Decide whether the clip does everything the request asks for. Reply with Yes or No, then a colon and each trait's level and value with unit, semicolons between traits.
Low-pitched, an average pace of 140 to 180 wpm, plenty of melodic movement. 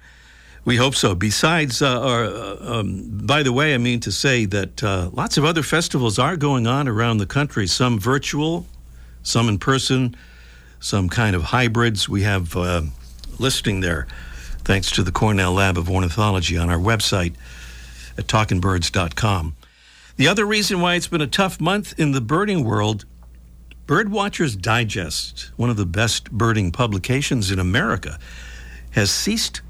Yes: low, 105 Hz; average, 160 wpm; wide, 7.5 semitones